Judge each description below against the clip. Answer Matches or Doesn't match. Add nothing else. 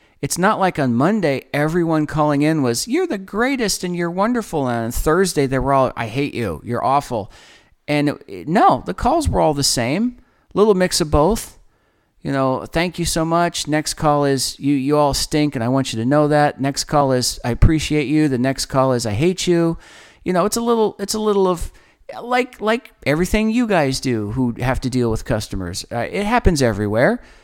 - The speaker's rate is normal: Doesn't match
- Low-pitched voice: Doesn't match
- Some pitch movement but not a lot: Doesn't match